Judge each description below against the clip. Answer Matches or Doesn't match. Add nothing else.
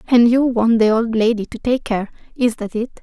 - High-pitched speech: Matches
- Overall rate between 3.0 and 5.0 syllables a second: Doesn't match